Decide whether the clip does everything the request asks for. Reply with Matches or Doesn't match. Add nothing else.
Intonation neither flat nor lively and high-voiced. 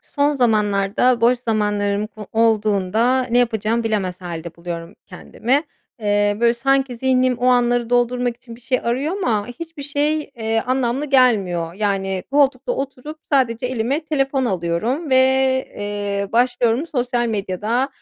Matches